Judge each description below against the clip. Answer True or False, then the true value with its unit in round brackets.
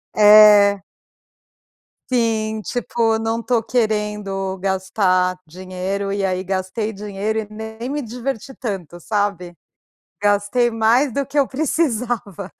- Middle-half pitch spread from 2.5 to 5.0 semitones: True (3.0 semitones)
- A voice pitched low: False (210 Hz)